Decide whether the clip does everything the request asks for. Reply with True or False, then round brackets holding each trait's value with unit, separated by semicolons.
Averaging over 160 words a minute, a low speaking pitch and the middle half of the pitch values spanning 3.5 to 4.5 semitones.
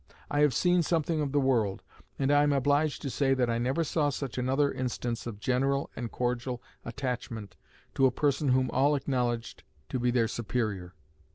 False (185 wpm; 130 Hz; 3.0 semitones)